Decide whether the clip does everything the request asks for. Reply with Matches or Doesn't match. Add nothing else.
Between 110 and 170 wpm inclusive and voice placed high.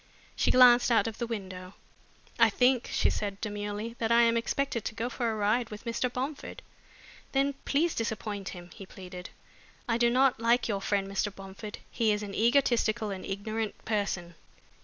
Doesn't match